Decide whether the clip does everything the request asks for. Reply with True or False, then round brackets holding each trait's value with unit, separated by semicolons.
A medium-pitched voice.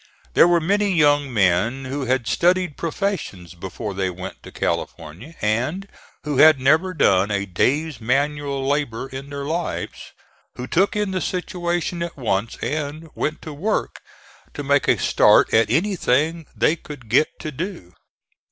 True (145 Hz)